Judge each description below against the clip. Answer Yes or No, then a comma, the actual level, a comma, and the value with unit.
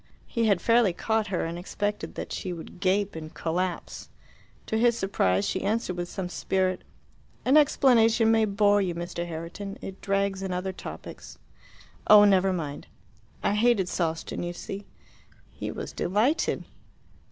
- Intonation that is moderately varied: Yes, average, 3.4 semitones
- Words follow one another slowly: No, average, 150 wpm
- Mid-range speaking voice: No, high, 195 Hz